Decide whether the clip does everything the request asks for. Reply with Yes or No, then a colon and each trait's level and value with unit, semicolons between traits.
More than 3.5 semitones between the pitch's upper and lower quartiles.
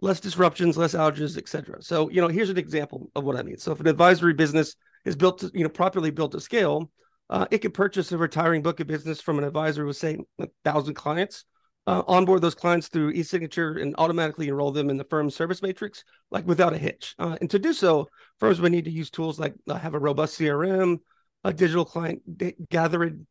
No: average, 2.9 semitones